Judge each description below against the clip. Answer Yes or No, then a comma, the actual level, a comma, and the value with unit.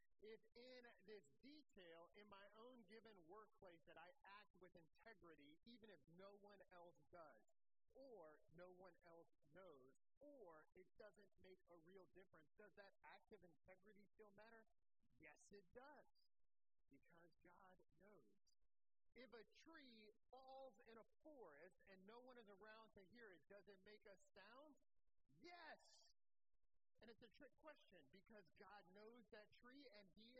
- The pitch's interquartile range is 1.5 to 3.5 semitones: No, average, 4.3 semitones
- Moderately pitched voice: No, high, 205 Hz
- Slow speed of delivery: No, average, 150 wpm